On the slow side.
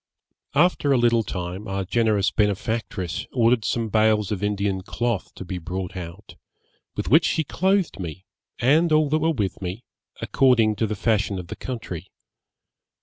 No: average, 160 wpm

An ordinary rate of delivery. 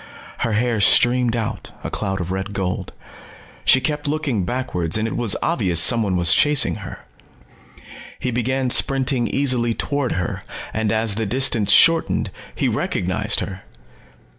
Yes: average, 145 wpm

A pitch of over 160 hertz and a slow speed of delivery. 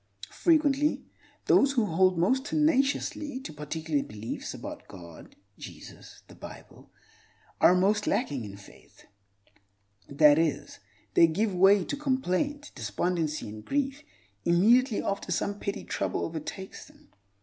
Yes: medium, 185 Hz; slow, 125 wpm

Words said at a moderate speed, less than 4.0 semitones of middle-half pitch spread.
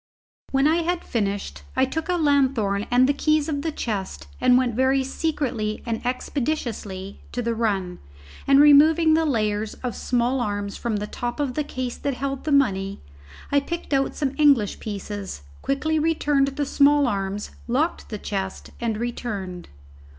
No: average, 165 wpm; wide, 5.4 semitones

